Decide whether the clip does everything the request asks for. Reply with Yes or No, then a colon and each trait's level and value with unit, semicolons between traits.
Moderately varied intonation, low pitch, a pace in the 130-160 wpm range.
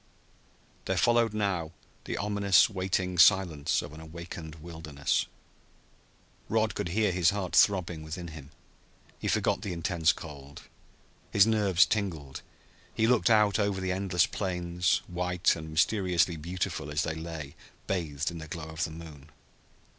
Yes: average, 3.5 semitones; very low, 85 Hz; average, 145 wpm